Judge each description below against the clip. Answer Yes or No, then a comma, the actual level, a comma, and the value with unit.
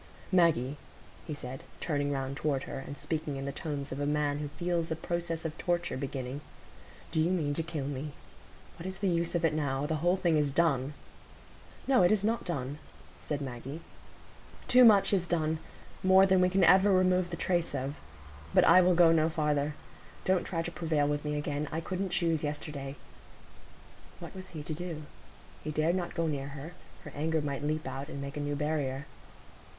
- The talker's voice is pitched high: No, medium, 155 Hz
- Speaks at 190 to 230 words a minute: Yes, average, 195 wpm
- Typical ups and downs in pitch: Yes, average, 3.3 semitones